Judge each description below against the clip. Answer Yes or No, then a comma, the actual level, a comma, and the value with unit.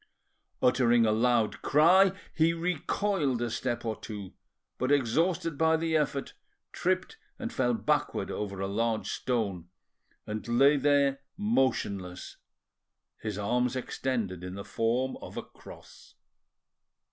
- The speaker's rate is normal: No, slow, 125 wpm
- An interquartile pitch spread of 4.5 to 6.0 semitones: Yes, wide, 5.5 semitones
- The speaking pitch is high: No, low, 125 Hz